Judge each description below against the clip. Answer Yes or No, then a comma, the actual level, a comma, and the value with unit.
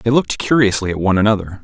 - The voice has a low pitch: Yes, low, 105 Hz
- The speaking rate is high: Yes, fast, 220 wpm